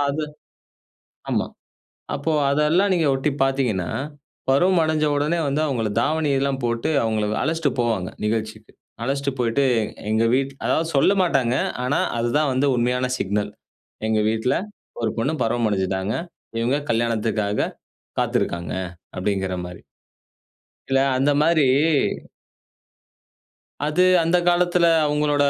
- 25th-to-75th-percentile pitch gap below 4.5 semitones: No, wide, 5.4 semitones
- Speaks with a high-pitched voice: No, low, 135 Hz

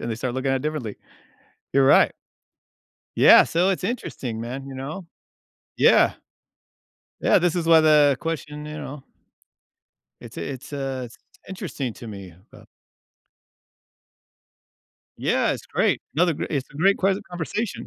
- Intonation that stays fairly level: No, average, 4.5 semitones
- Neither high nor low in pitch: Yes, medium, 150 Hz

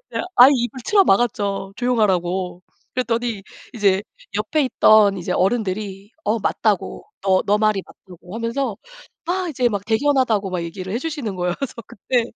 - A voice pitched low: No, high, 215 Hz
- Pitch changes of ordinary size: Yes, average, 4.1 semitones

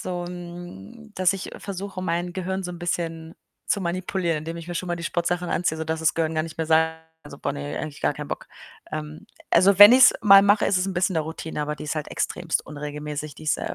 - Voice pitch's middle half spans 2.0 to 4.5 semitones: Yes, average, 2.7 semitones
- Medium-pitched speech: Yes, medium, 170 Hz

